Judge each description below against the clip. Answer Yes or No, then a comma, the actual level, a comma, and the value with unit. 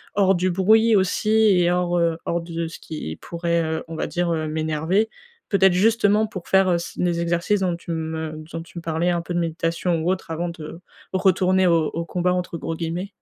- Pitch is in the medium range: Yes, medium, 175 Hz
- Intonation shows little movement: Yes, narrow, 2.2 semitones